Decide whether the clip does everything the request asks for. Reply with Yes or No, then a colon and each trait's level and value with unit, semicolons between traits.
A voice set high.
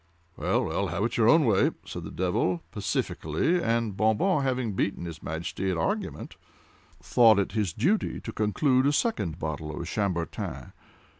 No: low, 105 Hz